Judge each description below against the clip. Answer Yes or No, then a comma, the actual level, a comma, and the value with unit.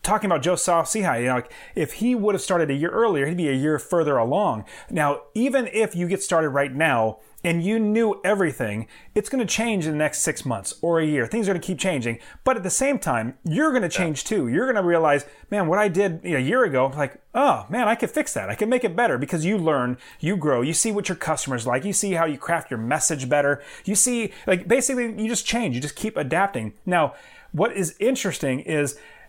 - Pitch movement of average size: No, wide, 6.6 semitones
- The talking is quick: Yes, fast, 240 wpm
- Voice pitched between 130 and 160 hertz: No, medium, 175 Hz